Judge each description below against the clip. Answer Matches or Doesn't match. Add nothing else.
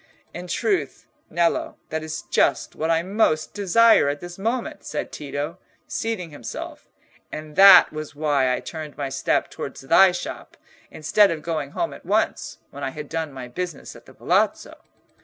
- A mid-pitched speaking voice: Matches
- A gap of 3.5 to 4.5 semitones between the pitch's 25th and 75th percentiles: Matches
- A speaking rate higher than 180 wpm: Doesn't match